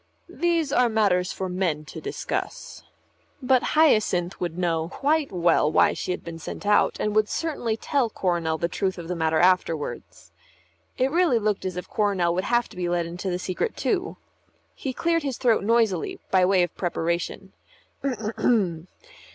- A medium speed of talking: Yes, average, 170 wpm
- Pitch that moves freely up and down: Yes, wide, 5.7 semitones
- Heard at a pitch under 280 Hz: Yes, high, 190 Hz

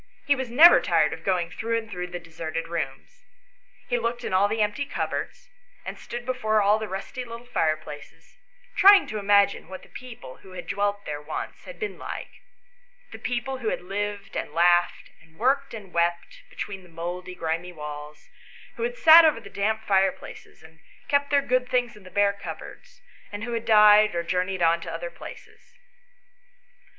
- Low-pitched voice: No, high, 200 Hz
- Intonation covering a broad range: Yes, wide, 5.8 semitones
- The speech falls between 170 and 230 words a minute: Yes, average, 185 wpm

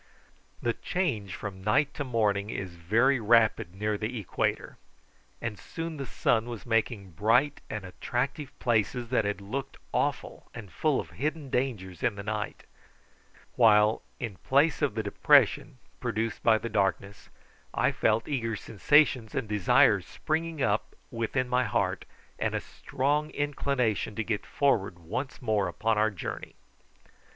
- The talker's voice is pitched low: Yes, low, 115 Hz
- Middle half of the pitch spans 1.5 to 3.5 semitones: No, average, 4.3 semitones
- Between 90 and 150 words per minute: Yes, average, 145 wpm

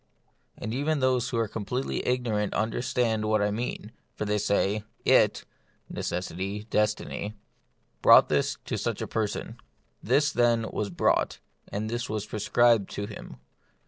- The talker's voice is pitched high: No, low, 110 Hz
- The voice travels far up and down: No, average, 2.7 semitones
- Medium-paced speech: Yes, average, 150 wpm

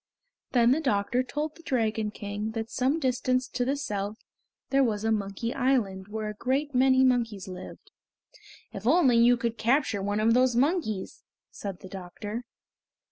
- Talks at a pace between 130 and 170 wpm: Yes, average, 165 wpm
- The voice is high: Yes, high, 235 Hz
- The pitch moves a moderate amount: Yes, average, 3.8 semitones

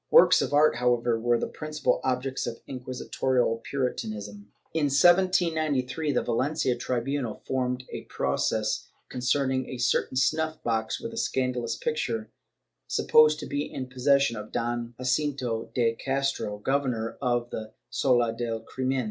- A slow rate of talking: No, average, 150 wpm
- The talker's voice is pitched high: No, low, 130 Hz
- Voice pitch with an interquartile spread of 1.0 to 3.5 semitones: Yes, average, 2.9 semitones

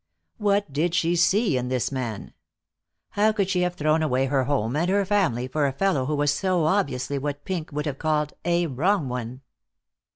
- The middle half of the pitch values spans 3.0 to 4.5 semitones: No, average, 5.2 semitones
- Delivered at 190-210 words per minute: Yes, average, 195 wpm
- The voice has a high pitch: No, medium, 155 Hz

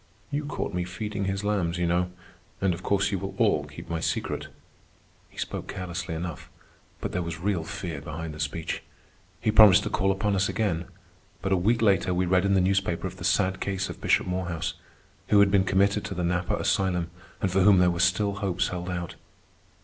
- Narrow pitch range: Yes, narrow, 2.0 semitones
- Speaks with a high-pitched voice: No, very low, 95 Hz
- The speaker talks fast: Yes, fast, 210 wpm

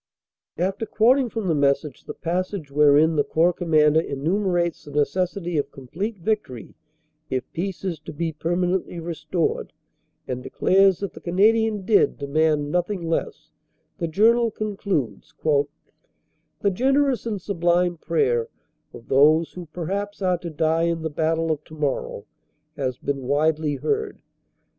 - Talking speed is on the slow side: No, average, 145 wpm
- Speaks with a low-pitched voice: No, medium, 170 Hz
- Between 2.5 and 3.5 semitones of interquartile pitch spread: No, average, 4.4 semitones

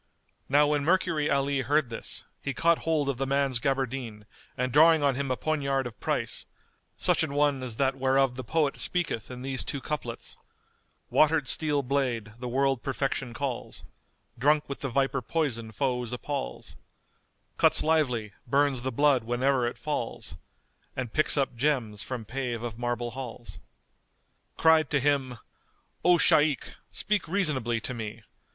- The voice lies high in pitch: No, low, 135 Hz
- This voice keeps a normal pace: Yes, average, 160 wpm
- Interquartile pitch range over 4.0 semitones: No, average, 3.2 semitones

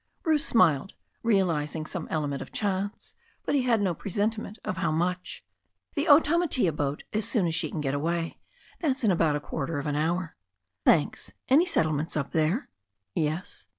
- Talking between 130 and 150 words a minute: No, average, 170 wpm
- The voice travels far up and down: Yes, wide, 6.1 semitones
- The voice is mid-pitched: Yes, medium, 175 Hz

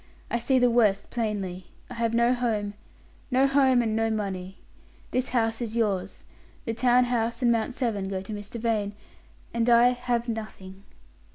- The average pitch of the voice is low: No, high, 230 Hz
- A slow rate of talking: No, average, 170 wpm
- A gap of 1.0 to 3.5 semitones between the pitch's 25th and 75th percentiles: Yes, average, 2.8 semitones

